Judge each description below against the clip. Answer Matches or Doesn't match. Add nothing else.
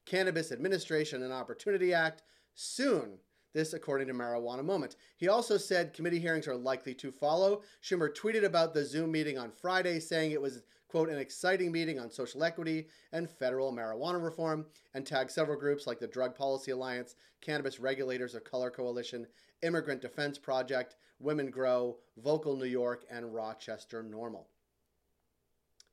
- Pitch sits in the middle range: Matches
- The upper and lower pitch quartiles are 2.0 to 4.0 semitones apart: Doesn't match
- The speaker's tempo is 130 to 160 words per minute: Matches